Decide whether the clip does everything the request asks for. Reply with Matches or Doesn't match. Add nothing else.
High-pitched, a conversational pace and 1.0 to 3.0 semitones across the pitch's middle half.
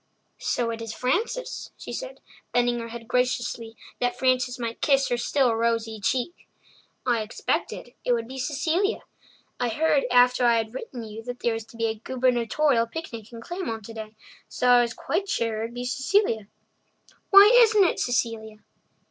Matches